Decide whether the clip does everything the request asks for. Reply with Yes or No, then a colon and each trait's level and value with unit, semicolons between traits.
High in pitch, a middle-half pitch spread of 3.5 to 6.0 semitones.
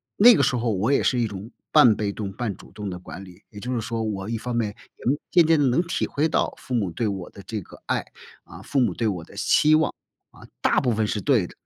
No: low, 115 Hz; average, 4.2 semitones